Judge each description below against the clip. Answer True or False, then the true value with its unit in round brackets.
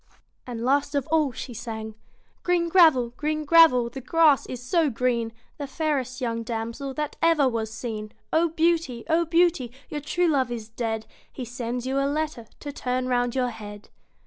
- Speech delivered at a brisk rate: False (180 wpm)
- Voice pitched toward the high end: True (260 Hz)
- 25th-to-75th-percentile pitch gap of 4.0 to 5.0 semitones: True (4.7 semitones)